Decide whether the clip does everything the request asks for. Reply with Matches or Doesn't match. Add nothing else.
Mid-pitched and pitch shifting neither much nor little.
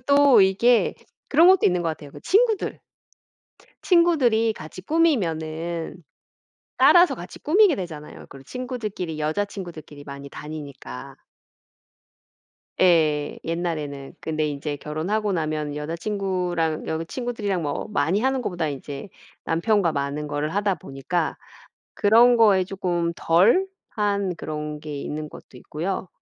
Doesn't match